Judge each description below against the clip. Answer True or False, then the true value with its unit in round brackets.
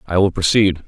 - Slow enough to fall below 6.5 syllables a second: True (5.3 syllables/s)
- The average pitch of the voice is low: True (95 Hz)